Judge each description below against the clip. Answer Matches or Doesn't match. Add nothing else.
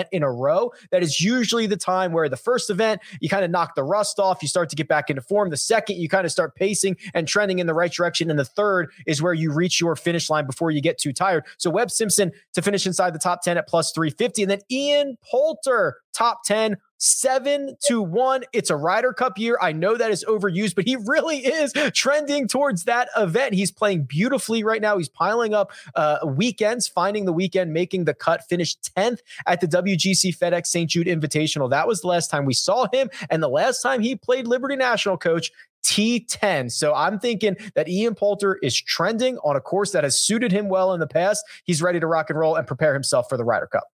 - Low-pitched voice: Doesn't match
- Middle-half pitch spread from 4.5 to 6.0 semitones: Matches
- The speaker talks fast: Matches